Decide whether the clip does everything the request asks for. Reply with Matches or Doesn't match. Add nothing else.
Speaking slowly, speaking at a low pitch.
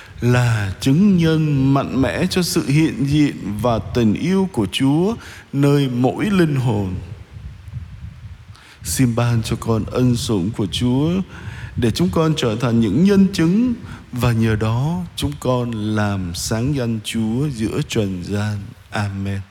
Matches